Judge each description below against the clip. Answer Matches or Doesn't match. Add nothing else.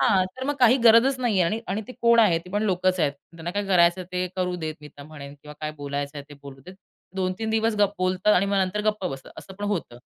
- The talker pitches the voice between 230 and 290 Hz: Doesn't match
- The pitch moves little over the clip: Doesn't match